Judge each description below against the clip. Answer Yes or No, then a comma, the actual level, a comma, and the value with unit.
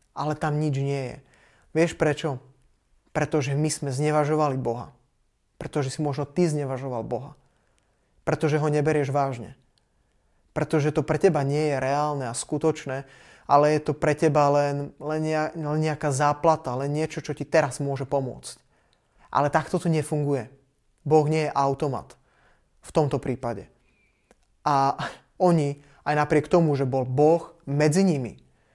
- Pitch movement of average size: No, narrow, 2.1 semitones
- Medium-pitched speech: Yes, medium, 150 Hz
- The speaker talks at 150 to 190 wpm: No, average, 140 wpm